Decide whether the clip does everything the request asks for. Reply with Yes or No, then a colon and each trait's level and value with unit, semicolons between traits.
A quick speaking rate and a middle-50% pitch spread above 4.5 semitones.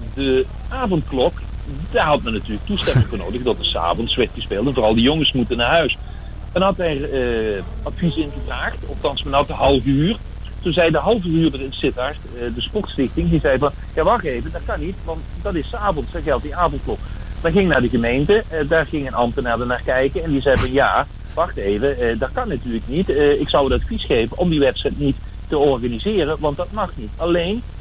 Yes: fast, 210 wpm; average, 5.1 semitones